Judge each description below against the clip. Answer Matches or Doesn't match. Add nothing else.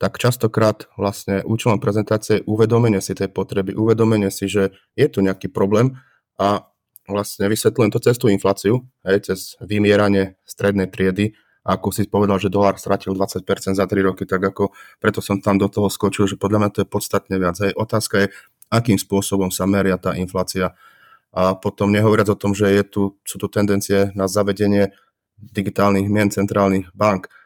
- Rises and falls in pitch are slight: Matches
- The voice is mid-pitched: Doesn't match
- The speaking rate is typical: Doesn't match